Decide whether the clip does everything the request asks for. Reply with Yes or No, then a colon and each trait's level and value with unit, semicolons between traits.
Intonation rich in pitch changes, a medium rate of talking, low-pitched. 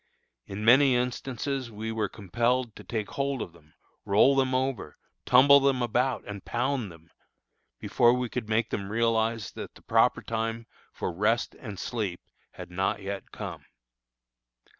No: average, 3.6 semitones; average, 155 wpm; low, 115 Hz